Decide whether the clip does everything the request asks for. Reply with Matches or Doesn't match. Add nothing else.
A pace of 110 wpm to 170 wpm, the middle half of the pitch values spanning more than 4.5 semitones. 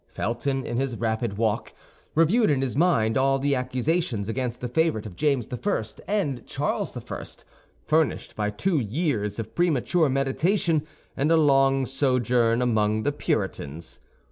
Matches